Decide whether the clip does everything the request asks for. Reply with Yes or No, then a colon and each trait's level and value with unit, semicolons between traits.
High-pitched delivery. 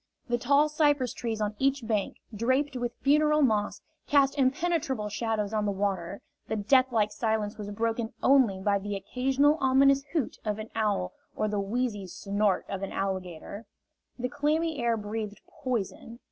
Yes: high, 225 Hz